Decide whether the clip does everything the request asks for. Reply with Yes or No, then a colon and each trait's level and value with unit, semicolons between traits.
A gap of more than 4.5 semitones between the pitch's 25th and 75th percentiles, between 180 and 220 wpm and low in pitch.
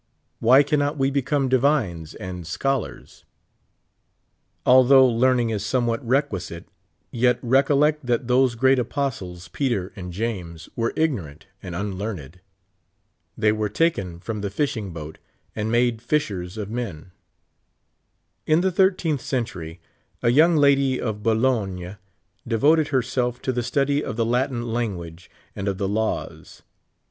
No: wide, 5.5 semitones; slow, 135 wpm; low, 120 Hz